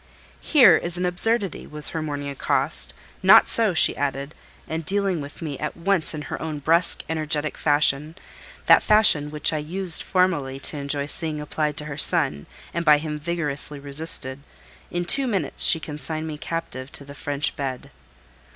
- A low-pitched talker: No, medium, 155 Hz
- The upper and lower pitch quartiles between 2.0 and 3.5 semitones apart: Yes, average, 2.9 semitones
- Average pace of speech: Yes, average, 165 wpm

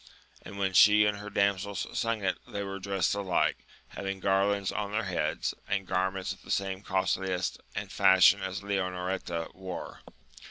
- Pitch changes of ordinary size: No, narrow, 1.2 semitones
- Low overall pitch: Yes, very low, 95 Hz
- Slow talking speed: No, average, 165 wpm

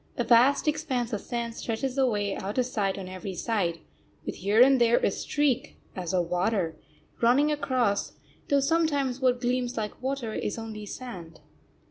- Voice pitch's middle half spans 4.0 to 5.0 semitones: Yes, average, 4.4 semitones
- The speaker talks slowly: No, average, 165 wpm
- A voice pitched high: Yes, high, 235 Hz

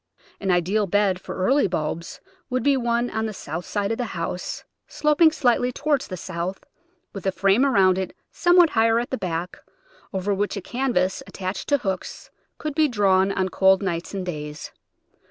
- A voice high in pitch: Yes, high, 200 Hz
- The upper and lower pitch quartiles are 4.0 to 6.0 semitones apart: Yes, average, 4.9 semitones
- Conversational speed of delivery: Yes, average, 180 wpm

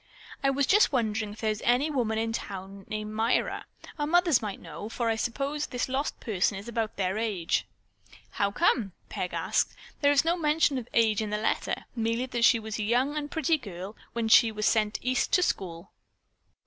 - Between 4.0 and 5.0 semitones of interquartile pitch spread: Yes, average, 4.4 semitones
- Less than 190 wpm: No, average, 200 wpm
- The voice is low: No, high, 225 Hz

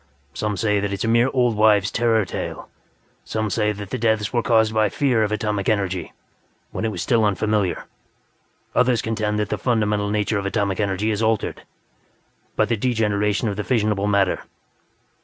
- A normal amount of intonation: No, narrow, 1.7 semitones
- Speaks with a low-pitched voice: Yes, low, 105 Hz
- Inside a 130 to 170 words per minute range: No, average, 180 wpm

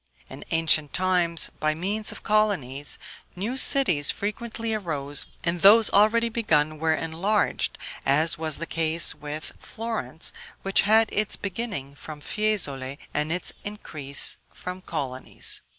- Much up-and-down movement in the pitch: Yes, wide, 6.0 semitones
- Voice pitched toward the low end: No, medium, 170 Hz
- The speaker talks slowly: Yes, slow, 130 wpm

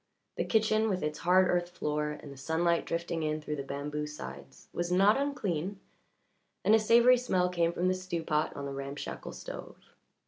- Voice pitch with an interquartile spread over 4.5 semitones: No, average, 3.9 semitones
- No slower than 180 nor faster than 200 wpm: Yes, average, 185 wpm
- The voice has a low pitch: No, medium, 170 Hz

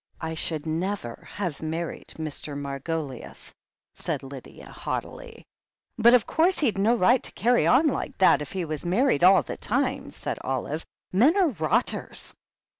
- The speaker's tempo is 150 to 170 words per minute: Yes, average, 155 wpm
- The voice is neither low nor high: Yes, medium, 175 Hz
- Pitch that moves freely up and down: Yes, wide, 7.7 semitones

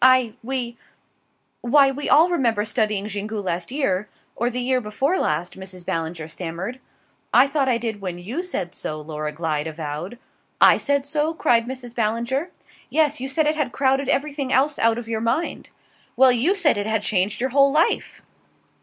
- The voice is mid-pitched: No, high, 235 Hz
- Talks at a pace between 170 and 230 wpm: Yes, average, 180 wpm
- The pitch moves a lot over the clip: Yes, wide, 6.0 semitones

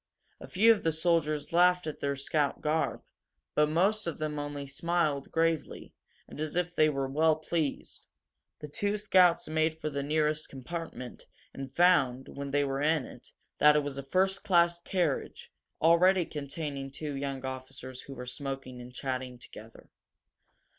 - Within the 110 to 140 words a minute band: No, average, 165 wpm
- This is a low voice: No, medium, 150 Hz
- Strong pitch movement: No, average, 3.6 semitones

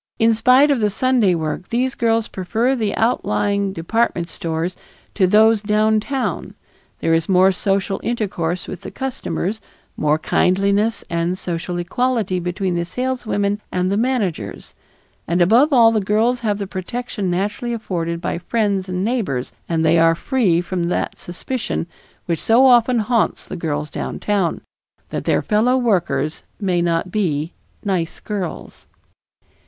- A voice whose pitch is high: Yes, high, 200 Hz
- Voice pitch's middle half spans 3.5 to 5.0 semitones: Yes, average, 4.7 semitones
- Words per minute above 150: No, average, 145 wpm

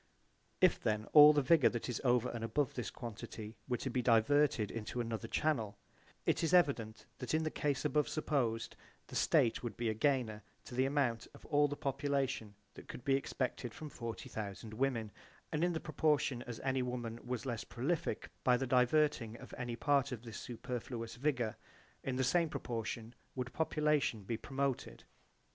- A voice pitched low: Yes, low, 125 Hz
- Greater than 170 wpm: Yes, average, 180 wpm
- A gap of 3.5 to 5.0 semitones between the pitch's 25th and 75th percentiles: Yes, average, 3.9 semitones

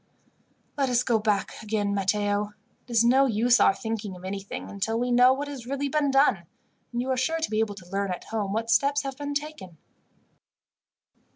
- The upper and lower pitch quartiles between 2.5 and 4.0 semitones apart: No, average, 4.7 semitones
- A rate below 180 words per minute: No, average, 200 wpm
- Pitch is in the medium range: No, high, 225 Hz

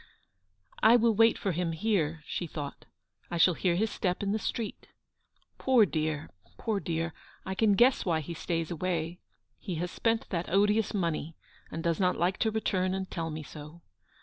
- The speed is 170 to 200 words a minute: Yes, average, 190 wpm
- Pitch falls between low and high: Yes, medium, 180 Hz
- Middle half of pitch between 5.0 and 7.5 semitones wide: No, average, 4.1 semitones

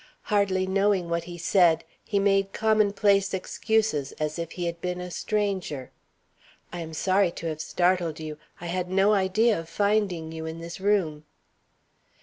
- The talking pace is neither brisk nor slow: Yes, average, 160 wpm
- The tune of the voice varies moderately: Yes, average, 3.2 semitones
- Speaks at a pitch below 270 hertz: Yes, medium, 185 Hz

